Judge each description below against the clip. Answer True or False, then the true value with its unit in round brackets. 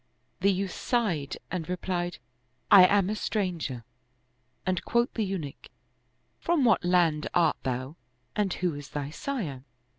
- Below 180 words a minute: True (160 wpm)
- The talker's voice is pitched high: False (180 Hz)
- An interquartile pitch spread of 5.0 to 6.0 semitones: True (5.4 semitones)